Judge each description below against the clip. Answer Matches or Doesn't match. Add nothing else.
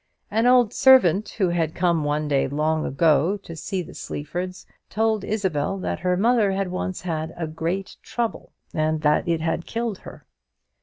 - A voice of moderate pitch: Matches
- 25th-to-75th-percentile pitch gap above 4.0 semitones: Matches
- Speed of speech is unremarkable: Matches